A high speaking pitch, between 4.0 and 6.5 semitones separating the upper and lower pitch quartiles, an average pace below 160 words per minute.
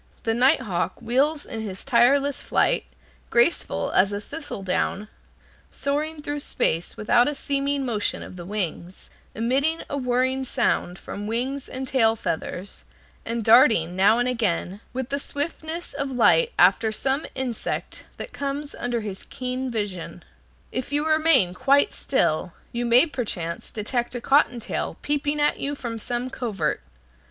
Yes: high, 245 Hz; average, 4.7 semitones; average, 150 wpm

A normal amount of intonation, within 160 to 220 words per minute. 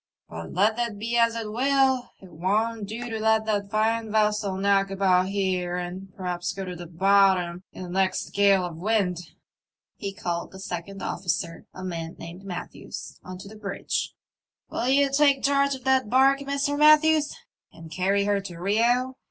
Yes: average, 4.1 semitones; average, 180 wpm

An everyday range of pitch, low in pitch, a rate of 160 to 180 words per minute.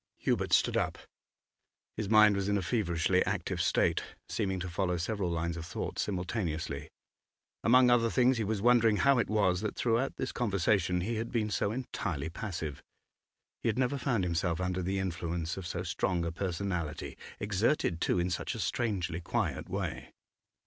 Yes: average, 4.2 semitones; very low, 95 Hz; average, 170 wpm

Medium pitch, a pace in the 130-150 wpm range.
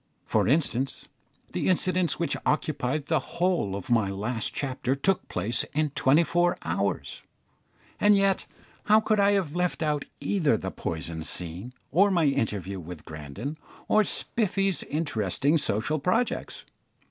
Yes: medium, 145 Hz; average, 140 wpm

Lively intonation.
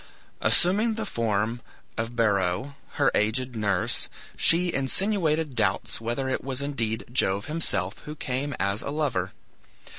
Yes: wide, 6.0 semitones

